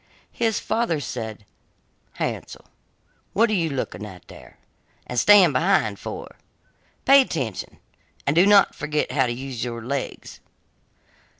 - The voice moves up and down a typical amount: No, wide, 8.7 semitones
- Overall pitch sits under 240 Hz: Yes, medium, 140 Hz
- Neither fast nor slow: No, slow, 130 wpm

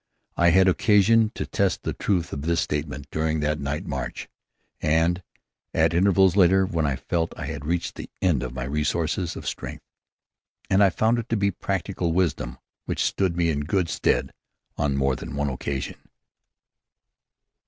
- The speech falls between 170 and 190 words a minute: Yes, average, 175 wpm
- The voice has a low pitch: Yes, very low, 85 Hz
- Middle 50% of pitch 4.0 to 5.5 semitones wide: Yes, average, 4.5 semitones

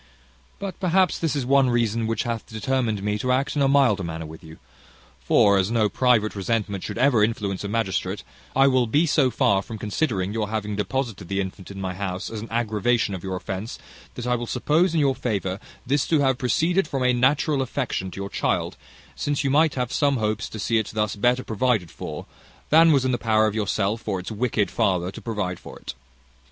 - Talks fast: Yes, fast, 215 wpm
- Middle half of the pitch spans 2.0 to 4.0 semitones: No, average, 4.7 semitones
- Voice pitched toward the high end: No, low, 115 Hz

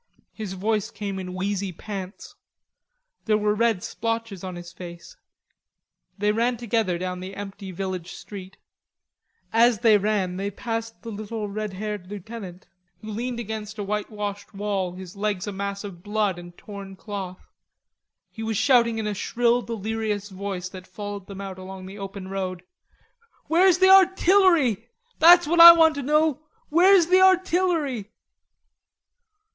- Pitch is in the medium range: No, high, 210 Hz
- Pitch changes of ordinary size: Yes, average, 3.4 semitones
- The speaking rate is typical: Yes, average, 150 wpm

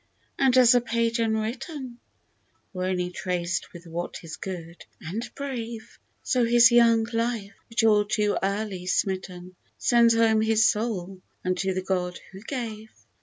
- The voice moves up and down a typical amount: Yes, average, 4.1 semitones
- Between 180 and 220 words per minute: No, average, 145 wpm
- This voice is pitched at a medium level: No, high, 220 Hz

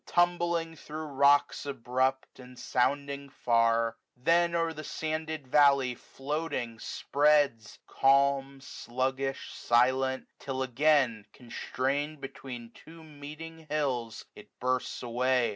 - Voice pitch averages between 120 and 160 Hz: Yes, low, 135 Hz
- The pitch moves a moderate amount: Yes, average, 3.2 semitones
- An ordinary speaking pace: No, slow, 110 wpm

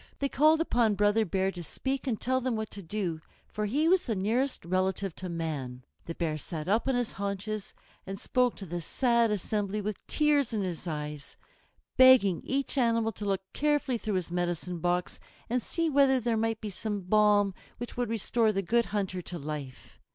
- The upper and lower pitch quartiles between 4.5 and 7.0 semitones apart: Yes, average, 5.1 semitones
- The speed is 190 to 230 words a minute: Yes, average, 195 wpm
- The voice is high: Yes, high, 210 Hz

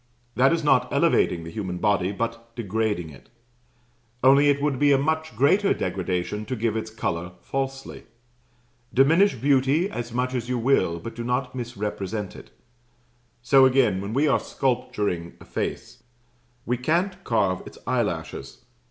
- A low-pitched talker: Yes, low, 120 Hz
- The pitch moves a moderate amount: Yes, average, 4.7 semitones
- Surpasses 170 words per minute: No, average, 150 wpm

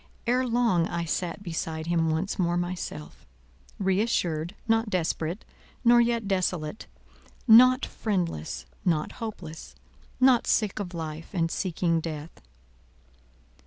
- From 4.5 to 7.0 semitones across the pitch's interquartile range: Yes, average, 5.2 semitones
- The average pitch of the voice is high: No, medium, 175 Hz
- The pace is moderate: No, slow, 115 wpm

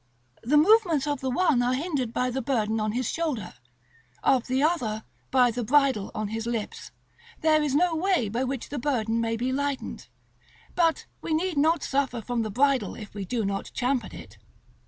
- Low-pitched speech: No, very high, 260 Hz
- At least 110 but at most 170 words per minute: No, average, 195 wpm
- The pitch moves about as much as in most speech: Yes, average, 4.6 semitones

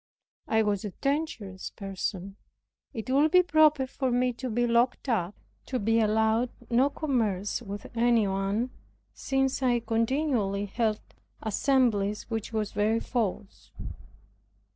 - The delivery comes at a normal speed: No, slow, 130 wpm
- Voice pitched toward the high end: Yes, high, 230 Hz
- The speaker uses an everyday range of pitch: Yes, average, 3.8 semitones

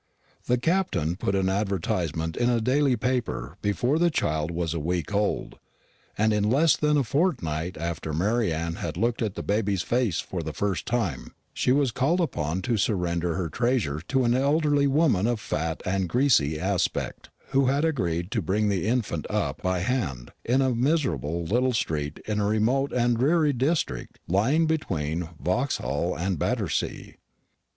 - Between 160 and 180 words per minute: Yes, average, 170 wpm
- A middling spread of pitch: No, wide, 7.3 semitones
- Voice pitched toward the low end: Yes, low, 105 Hz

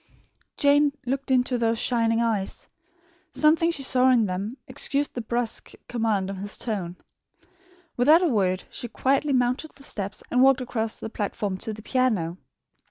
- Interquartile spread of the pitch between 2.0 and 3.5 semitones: No, average, 4.1 semitones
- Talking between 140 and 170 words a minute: Yes, average, 160 wpm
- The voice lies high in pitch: Yes, high, 240 Hz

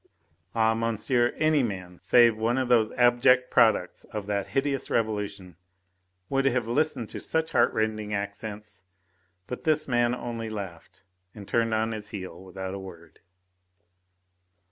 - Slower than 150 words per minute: Yes, average, 140 wpm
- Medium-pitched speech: No, low, 110 Hz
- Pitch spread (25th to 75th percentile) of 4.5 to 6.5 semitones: No, average, 3.3 semitones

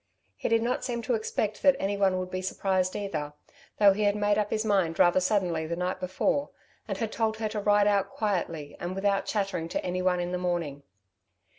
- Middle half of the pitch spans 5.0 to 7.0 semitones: No, average, 2.7 semitones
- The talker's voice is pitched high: Yes, high, 195 Hz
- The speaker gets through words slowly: No, fast, 205 wpm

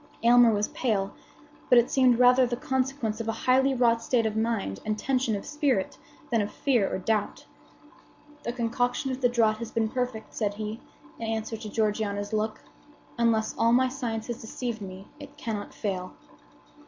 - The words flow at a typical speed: Yes, average, 180 wpm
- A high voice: Yes, high, 230 Hz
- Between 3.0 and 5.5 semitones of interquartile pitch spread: No, narrow, 2.6 semitones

